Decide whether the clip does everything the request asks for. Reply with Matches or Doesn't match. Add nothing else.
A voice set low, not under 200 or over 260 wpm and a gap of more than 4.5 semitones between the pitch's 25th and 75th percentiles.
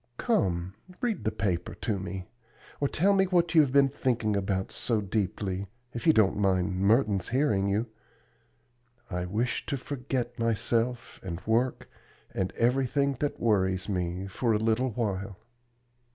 Doesn't match